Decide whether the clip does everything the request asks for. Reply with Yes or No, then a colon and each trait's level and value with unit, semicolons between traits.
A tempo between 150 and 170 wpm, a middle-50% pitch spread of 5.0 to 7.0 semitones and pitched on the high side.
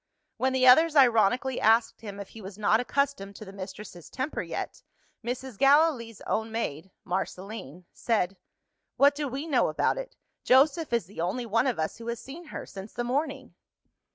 No: average, 180 wpm; average, 5.3 semitones; high, 235 Hz